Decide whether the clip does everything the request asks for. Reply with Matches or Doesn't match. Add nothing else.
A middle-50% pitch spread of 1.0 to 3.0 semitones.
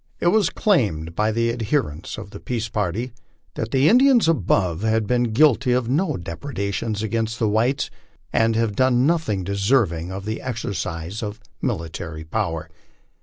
Doesn't match